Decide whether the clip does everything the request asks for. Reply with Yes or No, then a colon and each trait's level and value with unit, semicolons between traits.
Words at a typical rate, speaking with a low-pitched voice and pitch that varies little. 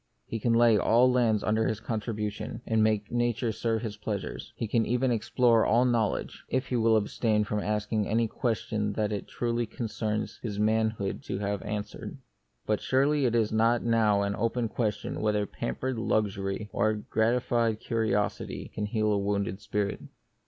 Yes: average, 170 wpm; low, 110 Hz; narrow, 2.0 semitones